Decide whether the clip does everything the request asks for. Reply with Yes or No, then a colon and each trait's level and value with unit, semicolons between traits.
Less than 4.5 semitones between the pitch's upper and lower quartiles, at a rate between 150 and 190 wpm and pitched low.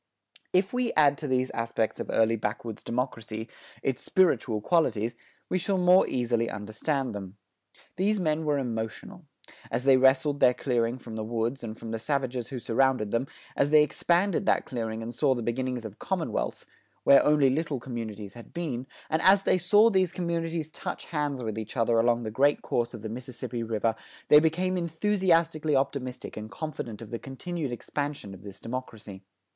No: wide, 5.6 semitones; average, 175 wpm; low, 130 Hz